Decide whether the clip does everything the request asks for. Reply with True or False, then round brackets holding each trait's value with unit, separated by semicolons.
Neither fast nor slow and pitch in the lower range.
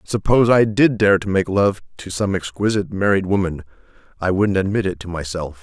True (180 wpm; 95 Hz)